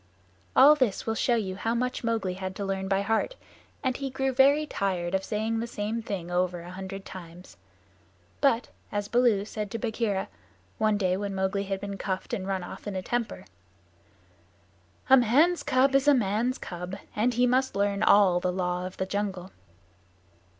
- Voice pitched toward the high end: Yes, high, 205 Hz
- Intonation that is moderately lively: Yes, average, 4.2 semitones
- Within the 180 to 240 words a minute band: Yes, average, 185 wpm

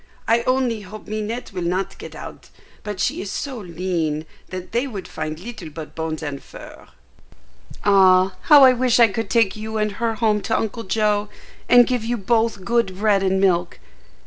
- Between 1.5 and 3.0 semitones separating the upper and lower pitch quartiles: No, average, 3.8 semitones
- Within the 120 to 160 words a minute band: No, average, 185 wpm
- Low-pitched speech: No, high, 210 Hz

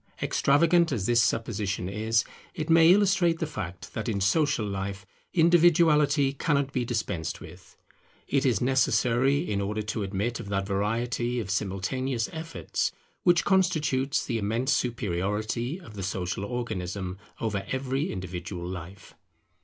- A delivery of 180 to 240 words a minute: No, slow, 135 wpm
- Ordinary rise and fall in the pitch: No, wide, 6.3 semitones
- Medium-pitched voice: No, low, 115 Hz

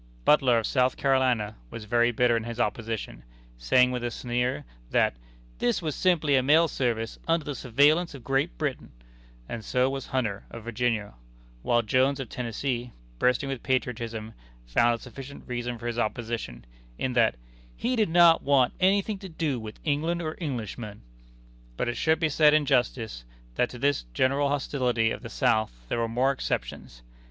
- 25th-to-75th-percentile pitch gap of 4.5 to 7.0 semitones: No, average, 3.5 semitones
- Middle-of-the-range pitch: No, low, 125 Hz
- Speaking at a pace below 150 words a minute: No, average, 175 wpm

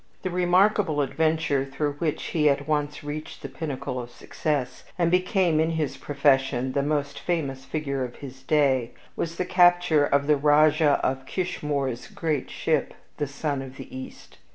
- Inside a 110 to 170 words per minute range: Yes, average, 165 wpm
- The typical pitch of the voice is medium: Yes, medium, 145 Hz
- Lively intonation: No, average, 3.0 semitones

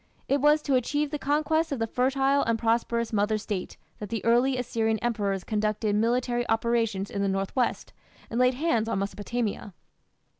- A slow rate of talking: No, average, 175 wpm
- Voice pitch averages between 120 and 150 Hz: No, high, 230 Hz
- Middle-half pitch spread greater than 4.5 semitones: No, average, 3.3 semitones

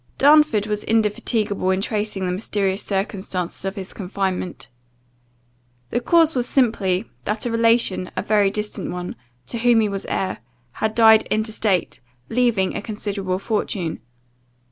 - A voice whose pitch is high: Yes, high, 210 Hz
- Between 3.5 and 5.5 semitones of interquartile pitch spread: No, average, 2.9 semitones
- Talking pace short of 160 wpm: Yes, average, 140 wpm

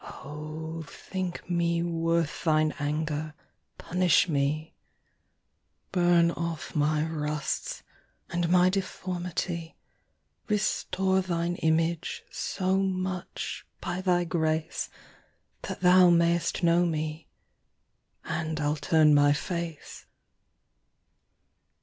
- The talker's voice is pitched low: No, medium, 170 Hz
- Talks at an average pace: No, slow, 80 wpm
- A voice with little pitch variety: Yes, narrow, 2.2 semitones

